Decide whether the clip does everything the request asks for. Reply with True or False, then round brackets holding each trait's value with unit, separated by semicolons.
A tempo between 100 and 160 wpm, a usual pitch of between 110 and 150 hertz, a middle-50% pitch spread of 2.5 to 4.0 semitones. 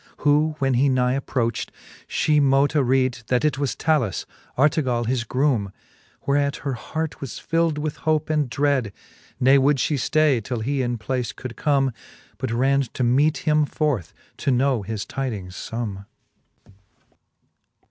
True (155 wpm; 135 Hz; 3.3 semitones)